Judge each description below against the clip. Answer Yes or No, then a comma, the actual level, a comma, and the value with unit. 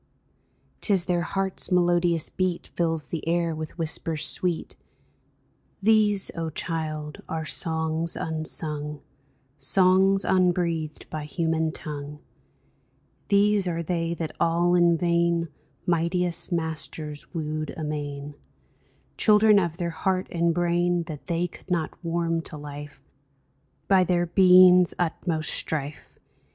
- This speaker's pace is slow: Yes, slow, 120 wpm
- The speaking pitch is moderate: Yes, medium, 170 Hz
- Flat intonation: Yes, narrow, 2.2 semitones